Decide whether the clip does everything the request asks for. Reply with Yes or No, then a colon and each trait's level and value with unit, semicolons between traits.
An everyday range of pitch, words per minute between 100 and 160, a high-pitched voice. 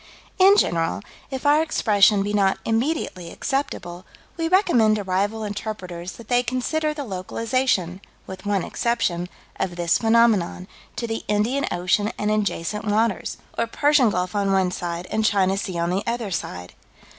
Yes: average, 4.3 semitones; average, 155 wpm; high, 210 Hz